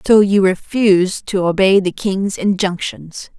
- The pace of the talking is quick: No, average, 140 wpm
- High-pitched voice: Yes, high, 195 Hz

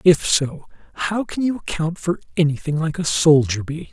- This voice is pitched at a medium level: Yes, medium, 155 Hz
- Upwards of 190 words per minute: No, average, 185 wpm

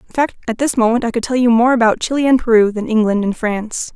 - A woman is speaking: Yes, female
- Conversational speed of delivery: No, fast, 275 wpm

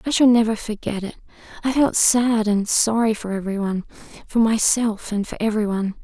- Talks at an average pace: Yes, average, 170 wpm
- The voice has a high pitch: Yes, high, 220 Hz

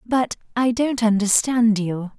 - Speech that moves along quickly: No, slow, 135 wpm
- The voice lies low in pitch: No, high, 225 Hz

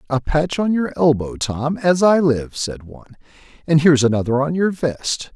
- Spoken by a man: Yes, male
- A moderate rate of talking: Yes, average, 190 wpm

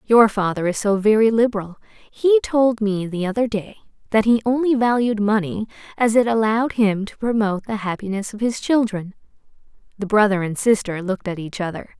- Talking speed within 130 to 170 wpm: No, average, 180 wpm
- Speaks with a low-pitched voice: No, high, 215 Hz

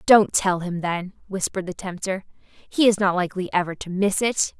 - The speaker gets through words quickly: No, average, 195 wpm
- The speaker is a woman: Yes, female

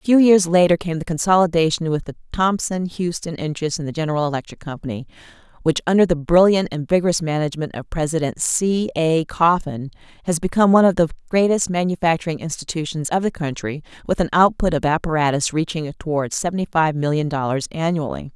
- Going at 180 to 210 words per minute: No, average, 170 wpm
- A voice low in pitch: No, medium, 165 Hz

